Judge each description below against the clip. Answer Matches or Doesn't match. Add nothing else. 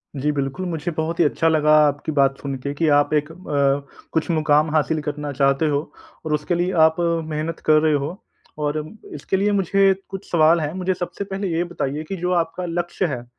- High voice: Doesn't match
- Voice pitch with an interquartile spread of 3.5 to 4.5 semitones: Doesn't match